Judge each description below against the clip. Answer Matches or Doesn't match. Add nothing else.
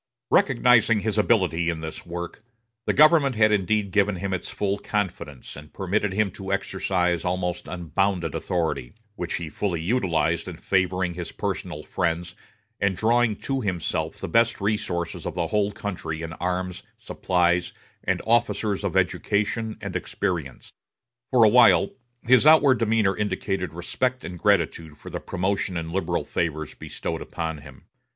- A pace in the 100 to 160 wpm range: Matches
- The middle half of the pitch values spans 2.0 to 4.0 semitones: Matches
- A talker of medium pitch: Doesn't match